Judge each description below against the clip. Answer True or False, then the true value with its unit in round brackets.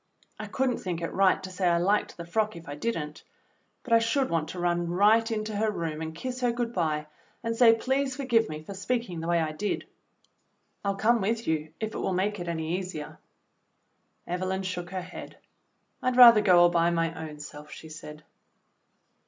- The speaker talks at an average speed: False (210 wpm)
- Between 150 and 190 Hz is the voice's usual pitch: True (185 Hz)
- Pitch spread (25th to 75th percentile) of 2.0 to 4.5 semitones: False (5.3 semitones)